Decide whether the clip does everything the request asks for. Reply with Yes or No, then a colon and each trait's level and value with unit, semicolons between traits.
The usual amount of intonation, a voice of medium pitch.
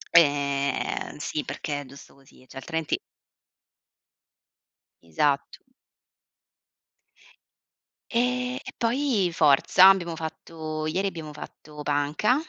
Yes: average, 5.0 semitones; medium, 155 Hz